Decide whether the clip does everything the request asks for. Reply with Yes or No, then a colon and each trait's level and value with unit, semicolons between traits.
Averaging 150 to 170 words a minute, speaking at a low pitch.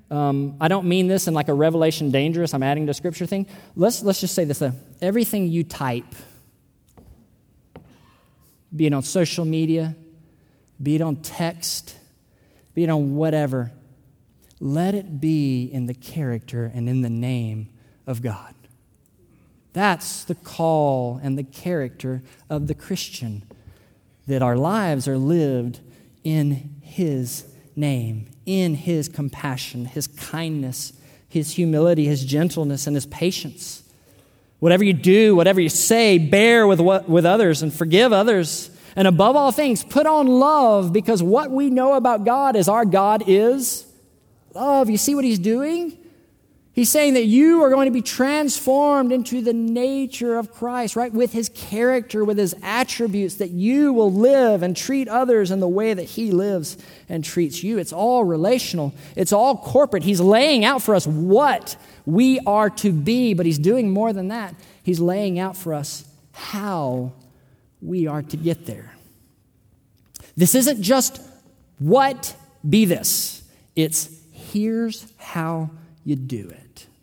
No: average, 155 wpm; medium, 170 Hz